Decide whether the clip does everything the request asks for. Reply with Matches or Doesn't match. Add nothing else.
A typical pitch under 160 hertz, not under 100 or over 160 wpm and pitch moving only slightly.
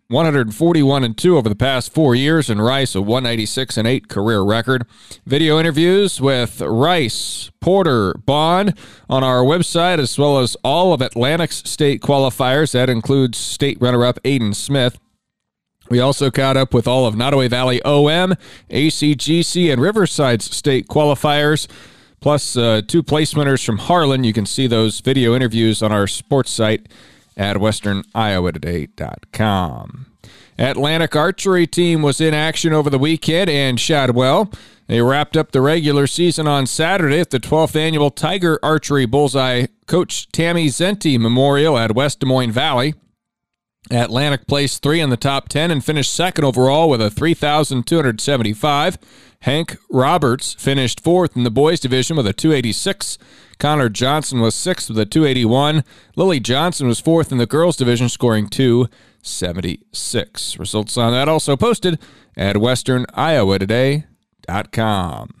Doesn't match